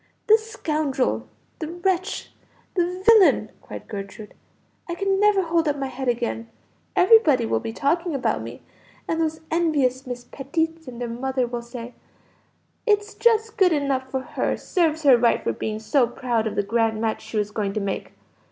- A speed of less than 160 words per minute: No, average, 175 wpm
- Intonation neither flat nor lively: No, wide, 6.5 semitones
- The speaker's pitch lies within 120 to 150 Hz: No, very high, 275 Hz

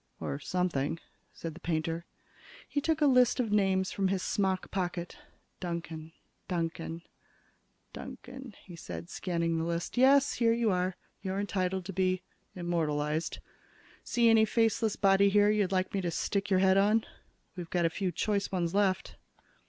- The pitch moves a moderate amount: Yes, average, 3.4 semitones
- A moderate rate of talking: Yes, average, 160 wpm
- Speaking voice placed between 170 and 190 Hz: Yes, medium, 185 Hz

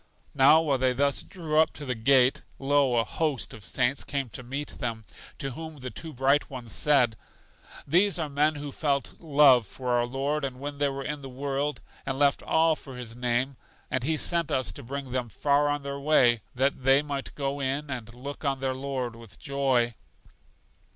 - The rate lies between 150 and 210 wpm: Yes, average, 200 wpm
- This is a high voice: No, low, 135 Hz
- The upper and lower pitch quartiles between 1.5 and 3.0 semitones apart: Yes, narrow, 2.4 semitones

